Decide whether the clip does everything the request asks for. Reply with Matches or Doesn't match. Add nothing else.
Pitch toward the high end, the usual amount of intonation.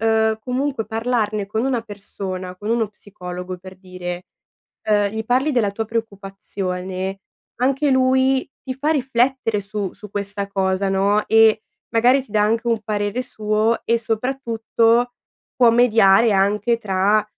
Matches